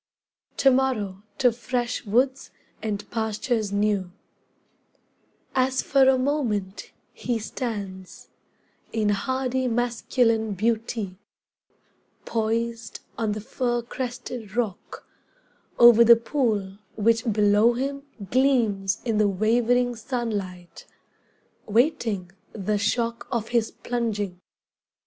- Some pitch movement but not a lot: Yes, average, 3.0 semitones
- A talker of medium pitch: No, high, 230 Hz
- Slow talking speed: Yes, slow, 95 wpm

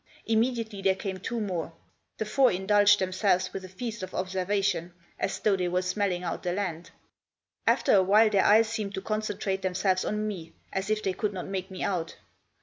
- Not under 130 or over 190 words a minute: No, average, 200 wpm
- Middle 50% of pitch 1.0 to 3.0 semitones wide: Yes, narrow, 2.4 semitones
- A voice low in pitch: No, high, 195 Hz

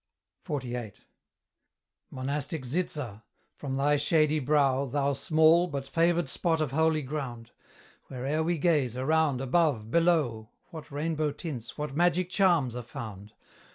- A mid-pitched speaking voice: Yes, medium, 145 Hz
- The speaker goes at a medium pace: No, slow, 125 wpm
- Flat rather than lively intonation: No, average, 3.7 semitones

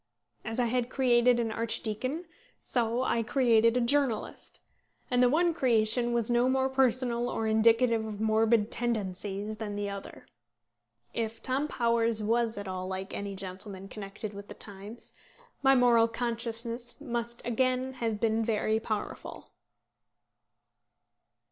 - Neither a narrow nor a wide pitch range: No, narrow, 2.3 semitones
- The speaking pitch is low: No, high, 230 Hz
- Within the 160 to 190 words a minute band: No, average, 140 wpm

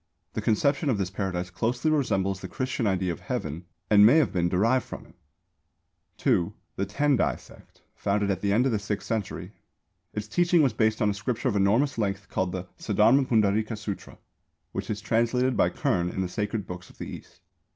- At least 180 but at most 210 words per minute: Yes, average, 195 wpm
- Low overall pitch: Yes, low, 105 Hz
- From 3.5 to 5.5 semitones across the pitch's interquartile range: Yes, average, 3.8 semitones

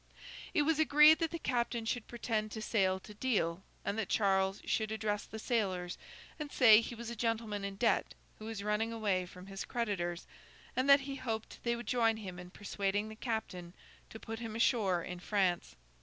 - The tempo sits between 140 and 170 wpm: No, average, 195 wpm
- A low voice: No, high, 220 Hz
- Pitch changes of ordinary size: Yes, average, 3.3 semitones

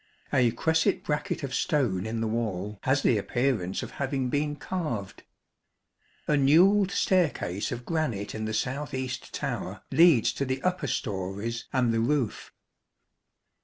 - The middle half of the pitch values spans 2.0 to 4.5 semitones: No, average, 5.2 semitones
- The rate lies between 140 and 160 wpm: Yes, average, 145 wpm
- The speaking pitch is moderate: No, low, 130 Hz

